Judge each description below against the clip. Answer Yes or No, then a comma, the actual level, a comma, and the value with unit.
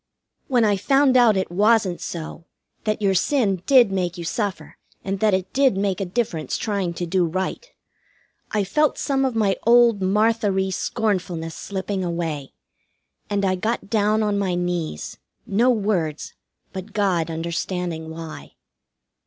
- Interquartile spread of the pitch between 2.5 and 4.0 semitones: Yes, average, 3.7 semitones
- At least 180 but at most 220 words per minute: No, average, 155 wpm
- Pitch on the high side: Yes, high, 195 Hz